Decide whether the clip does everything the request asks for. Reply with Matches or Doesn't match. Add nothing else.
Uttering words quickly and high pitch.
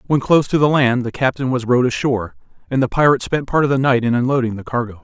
Doesn't match